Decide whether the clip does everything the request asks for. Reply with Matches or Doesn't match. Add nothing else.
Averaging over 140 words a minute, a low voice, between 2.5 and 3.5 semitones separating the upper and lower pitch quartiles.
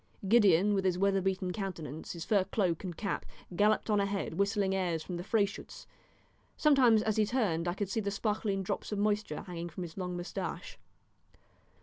Doesn't match